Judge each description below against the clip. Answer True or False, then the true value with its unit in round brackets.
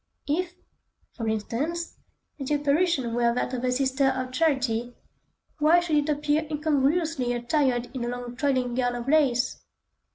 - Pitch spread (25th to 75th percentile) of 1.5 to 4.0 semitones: True (3.6 semitones)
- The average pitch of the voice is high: True (265 Hz)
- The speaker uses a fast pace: False (150 wpm)